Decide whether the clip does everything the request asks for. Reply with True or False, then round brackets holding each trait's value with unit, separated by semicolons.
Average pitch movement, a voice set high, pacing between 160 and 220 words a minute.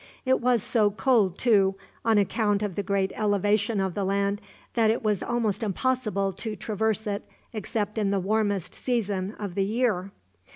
False (2.1 semitones; 205 Hz; 170 wpm)